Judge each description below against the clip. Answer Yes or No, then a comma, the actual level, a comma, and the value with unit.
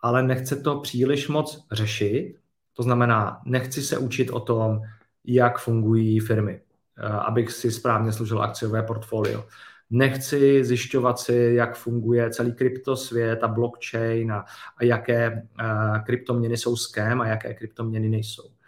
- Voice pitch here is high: No, low, 120 Hz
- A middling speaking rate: Yes, average, 130 wpm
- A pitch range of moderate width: No, narrow, 2.0 semitones